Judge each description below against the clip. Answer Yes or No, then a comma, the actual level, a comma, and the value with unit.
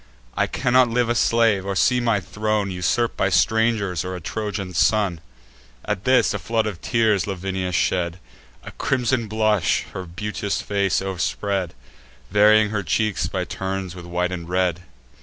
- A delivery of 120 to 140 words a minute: No, average, 160 wpm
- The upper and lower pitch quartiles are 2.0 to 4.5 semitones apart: Yes, average, 3.1 semitones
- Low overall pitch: Yes, low, 100 Hz